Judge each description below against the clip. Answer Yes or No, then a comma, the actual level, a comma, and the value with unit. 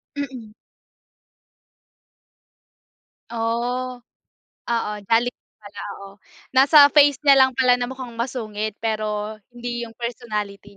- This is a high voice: Yes, high, 235 Hz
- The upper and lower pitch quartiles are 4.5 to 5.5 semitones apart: No, average, 2.9 semitones